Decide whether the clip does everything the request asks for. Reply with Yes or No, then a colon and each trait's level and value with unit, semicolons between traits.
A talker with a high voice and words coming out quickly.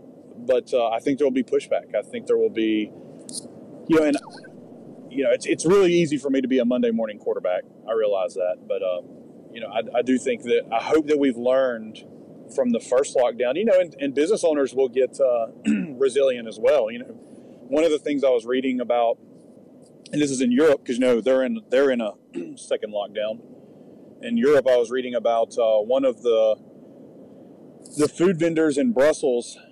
Yes: high, 240 Hz; fast, 210 wpm